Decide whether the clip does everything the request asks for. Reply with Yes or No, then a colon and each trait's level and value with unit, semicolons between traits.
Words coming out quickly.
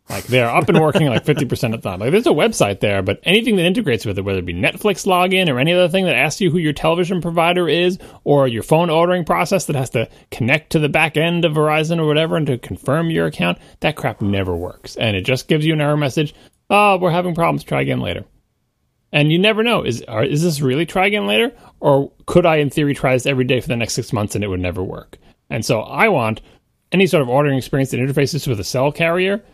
Yes: fast, 250 wpm